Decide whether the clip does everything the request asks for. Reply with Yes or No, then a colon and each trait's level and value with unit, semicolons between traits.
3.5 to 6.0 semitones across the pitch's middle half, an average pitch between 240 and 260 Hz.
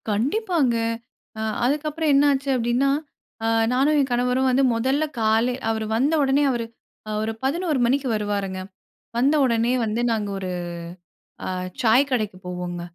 Yes: average, 4.0 semitones; very high, 250 Hz